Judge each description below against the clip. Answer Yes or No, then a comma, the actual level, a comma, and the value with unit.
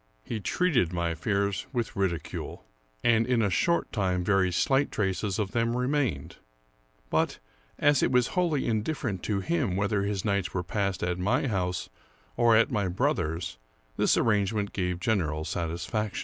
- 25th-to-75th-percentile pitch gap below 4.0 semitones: No, average, 4.4 semitones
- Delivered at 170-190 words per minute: No, average, 155 wpm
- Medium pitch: No, low, 100 Hz